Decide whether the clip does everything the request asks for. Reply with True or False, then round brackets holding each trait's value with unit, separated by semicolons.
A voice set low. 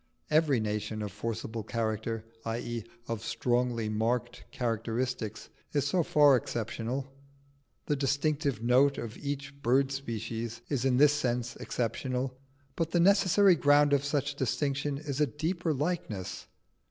True (130 Hz)